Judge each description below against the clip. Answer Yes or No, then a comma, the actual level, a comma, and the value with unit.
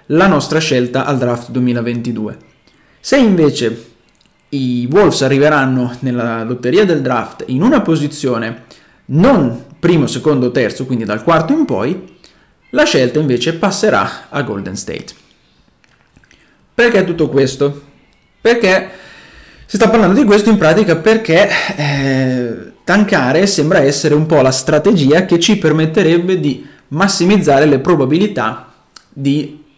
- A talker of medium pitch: Yes, medium, 150 Hz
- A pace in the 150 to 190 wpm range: No, average, 125 wpm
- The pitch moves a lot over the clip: Yes, wide, 6.5 semitones